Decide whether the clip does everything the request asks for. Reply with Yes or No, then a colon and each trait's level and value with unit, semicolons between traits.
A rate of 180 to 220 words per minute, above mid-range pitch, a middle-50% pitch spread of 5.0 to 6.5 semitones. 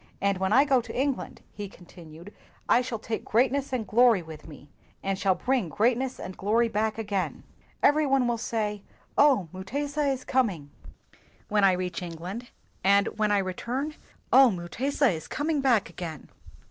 No: average, 170 wpm; high, 215 Hz; wide, 5.6 semitones